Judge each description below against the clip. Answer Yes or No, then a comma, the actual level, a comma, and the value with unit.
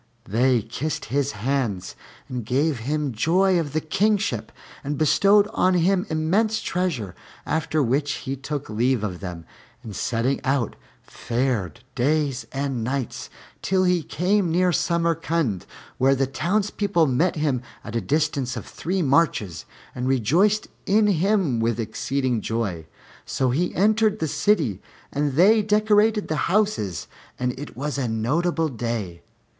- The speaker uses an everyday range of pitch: No, wide, 6.7 semitones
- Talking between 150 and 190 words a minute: No, average, 140 wpm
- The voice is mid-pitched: Yes, medium, 145 Hz